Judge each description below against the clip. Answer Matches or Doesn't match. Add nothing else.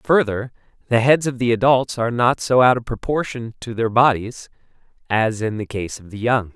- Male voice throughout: Matches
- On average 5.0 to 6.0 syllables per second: Matches